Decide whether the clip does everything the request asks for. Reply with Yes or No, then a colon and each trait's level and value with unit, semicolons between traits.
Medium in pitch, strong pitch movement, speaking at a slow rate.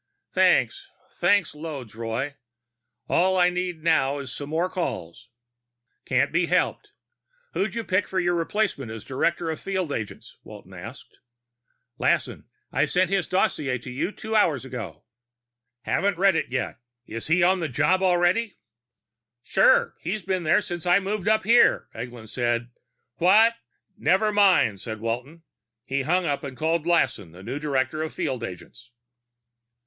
No: medium, 160 Hz; wide, 6.5 semitones; average, 155 wpm